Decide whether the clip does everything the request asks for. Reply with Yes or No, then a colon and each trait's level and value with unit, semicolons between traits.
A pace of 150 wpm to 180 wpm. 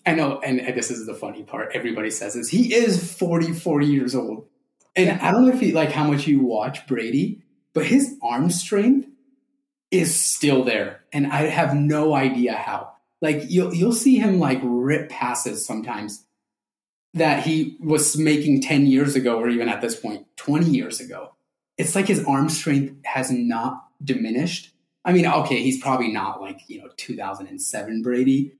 Yes: average, 175 wpm